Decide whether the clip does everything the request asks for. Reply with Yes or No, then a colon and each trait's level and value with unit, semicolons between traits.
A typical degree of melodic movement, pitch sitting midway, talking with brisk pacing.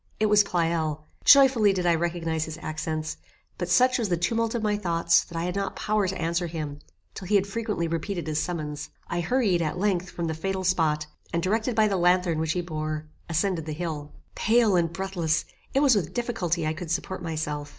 Yes: average, 3.8 semitones; medium, 175 Hz; fast, 210 wpm